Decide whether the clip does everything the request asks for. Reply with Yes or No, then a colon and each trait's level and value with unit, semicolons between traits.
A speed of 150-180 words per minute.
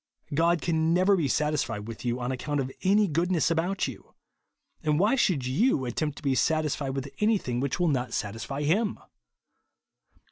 Yes: average, 170 wpm